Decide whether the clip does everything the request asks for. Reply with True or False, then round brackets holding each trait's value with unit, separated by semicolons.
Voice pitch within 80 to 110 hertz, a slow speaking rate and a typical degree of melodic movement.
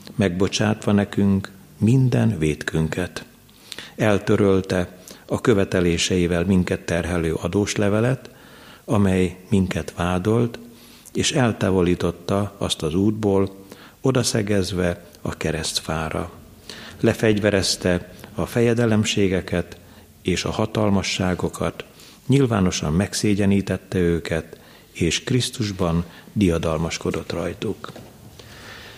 True (95 Hz; 70 wpm; 3.4 semitones)